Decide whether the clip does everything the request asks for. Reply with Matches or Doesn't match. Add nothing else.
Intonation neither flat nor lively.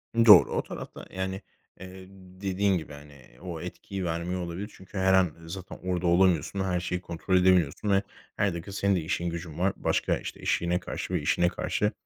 Doesn't match